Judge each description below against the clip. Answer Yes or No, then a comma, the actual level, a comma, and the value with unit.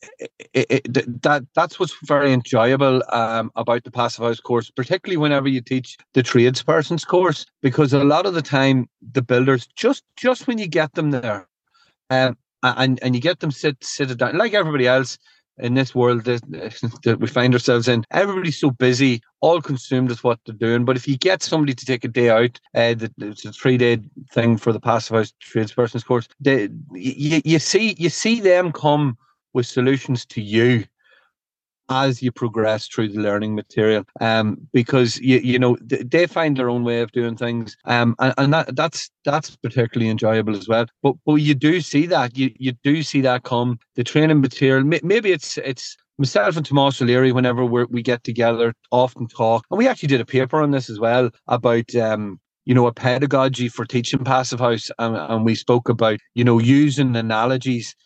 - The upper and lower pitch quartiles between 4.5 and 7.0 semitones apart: No, average, 3.3 semitones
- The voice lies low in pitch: Yes, low, 130 Hz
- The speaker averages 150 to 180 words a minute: No, average, 195 wpm